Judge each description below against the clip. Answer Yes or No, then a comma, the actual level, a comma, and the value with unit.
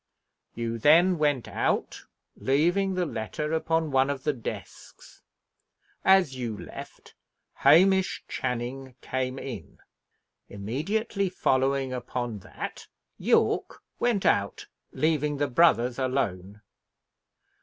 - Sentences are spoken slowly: Yes, slow, 100 wpm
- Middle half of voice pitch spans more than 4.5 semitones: Yes, average, 5.1 semitones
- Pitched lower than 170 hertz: Yes, low, 135 Hz